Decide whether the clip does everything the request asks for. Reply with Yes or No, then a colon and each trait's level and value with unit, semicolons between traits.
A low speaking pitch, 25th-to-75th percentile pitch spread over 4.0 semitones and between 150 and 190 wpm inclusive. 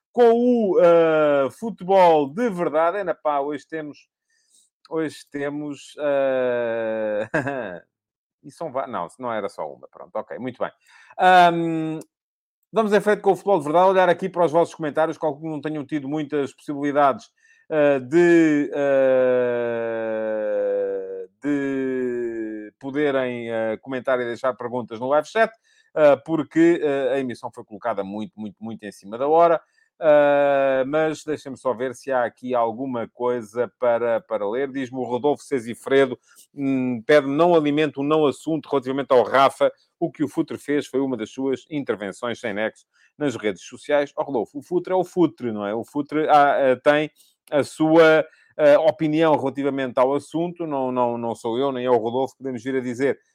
No: medium, 145 Hz; average, 4.7 semitones; average, 165 wpm